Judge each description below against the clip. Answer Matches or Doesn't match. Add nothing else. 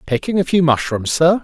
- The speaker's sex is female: Doesn't match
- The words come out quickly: Matches